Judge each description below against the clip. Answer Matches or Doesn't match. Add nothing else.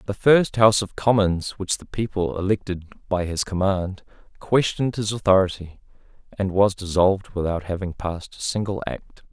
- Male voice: Matches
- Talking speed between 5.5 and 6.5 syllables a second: Doesn't match